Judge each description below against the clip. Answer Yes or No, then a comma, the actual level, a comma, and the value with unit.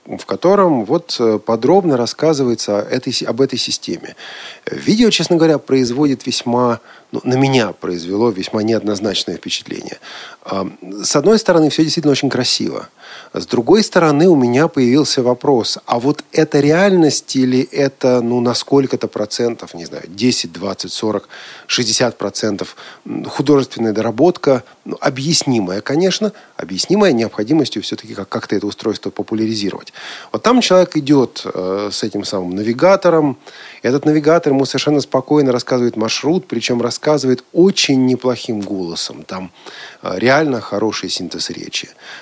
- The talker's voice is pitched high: No, low, 125 Hz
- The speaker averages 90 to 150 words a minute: Yes, average, 130 wpm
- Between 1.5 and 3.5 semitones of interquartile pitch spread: No, average, 5.0 semitones